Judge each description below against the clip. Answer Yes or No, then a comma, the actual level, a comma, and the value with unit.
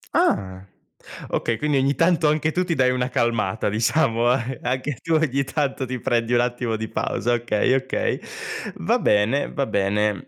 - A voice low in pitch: Yes, low, 125 Hz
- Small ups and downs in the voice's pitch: No, average, 3.8 semitones